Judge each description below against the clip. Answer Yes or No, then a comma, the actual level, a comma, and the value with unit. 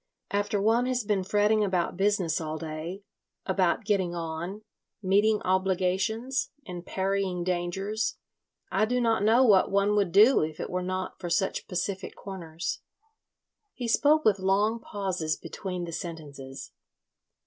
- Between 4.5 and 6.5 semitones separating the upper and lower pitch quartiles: No, average, 3.1 semitones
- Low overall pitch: No, high, 190 Hz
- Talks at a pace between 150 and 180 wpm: No, average, 140 wpm